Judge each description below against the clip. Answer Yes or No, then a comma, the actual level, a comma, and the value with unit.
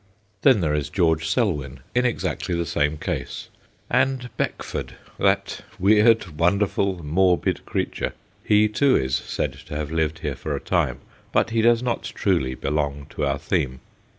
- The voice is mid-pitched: No, very low, 85 Hz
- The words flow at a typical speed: Yes, average, 155 wpm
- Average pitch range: No, wide, 6.5 semitones